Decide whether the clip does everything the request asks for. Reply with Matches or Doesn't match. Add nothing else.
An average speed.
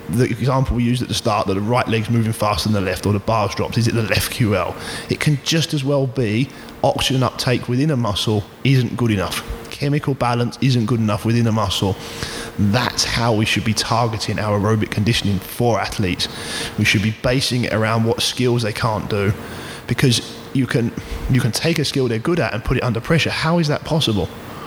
Doesn't match